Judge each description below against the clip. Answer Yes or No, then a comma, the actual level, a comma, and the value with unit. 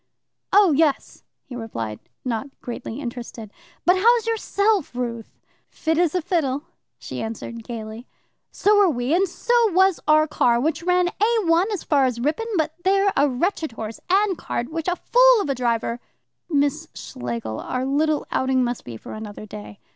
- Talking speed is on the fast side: No, average, 175 wpm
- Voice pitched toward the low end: No, very high, 290 Hz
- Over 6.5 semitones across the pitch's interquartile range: Yes, wide, 7.5 semitones